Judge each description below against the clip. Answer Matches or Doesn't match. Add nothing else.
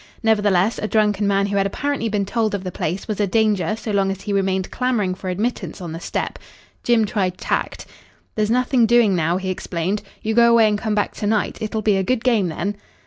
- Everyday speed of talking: Doesn't match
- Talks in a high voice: Matches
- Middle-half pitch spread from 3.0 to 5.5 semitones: Doesn't match